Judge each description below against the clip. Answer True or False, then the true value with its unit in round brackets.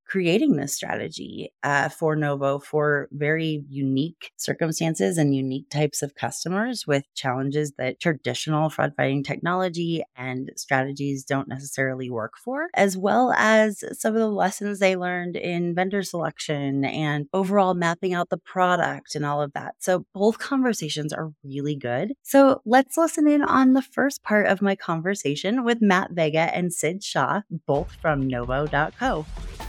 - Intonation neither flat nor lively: False (5.7 semitones)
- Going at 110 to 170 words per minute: True (155 wpm)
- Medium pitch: True (160 Hz)